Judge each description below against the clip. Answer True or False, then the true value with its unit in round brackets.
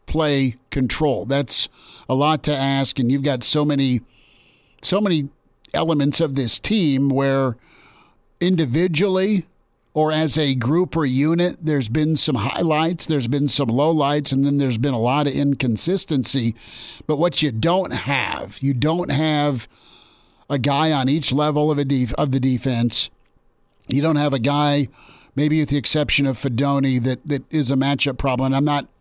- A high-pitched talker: False (140 Hz)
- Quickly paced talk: False (170 wpm)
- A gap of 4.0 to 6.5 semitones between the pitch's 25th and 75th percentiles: False (2.6 semitones)